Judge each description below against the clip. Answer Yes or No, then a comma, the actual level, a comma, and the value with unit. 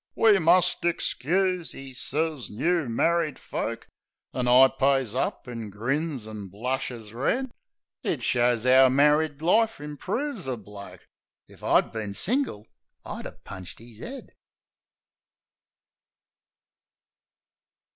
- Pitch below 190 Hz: Yes, low, 135 Hz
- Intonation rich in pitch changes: Yes, wide, 6.5 semitones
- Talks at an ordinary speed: No, slow, 115 wpm